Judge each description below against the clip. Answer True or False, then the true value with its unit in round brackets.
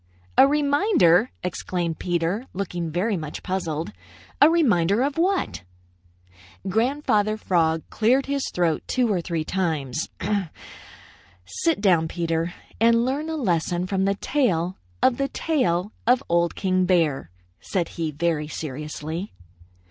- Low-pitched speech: False (185 Hz)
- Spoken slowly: True (125 wpm)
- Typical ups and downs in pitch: False (6.8 semitones)